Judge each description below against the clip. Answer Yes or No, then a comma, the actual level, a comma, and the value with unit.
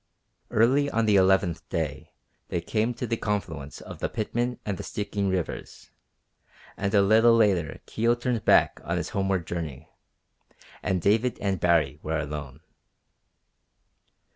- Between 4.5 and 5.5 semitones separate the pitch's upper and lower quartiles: Yes, average, 5.2 semitones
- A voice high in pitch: No, low, 100 Hz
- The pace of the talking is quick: No, average, 140 wpm